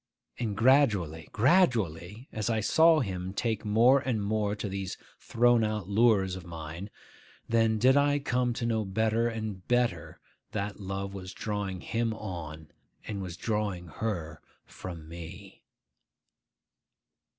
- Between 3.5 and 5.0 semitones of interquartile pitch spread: Yes, average, 3.8 semitones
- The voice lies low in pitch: Yes, low, 105 Hz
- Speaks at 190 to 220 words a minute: No, slow, 135 wpm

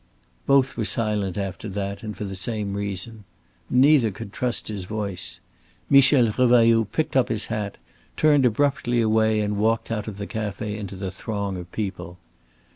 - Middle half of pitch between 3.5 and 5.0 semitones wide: No, average, 2.8 semitones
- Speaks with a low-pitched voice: Yes, low, 110 Hz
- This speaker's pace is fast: No, average, 165 wpm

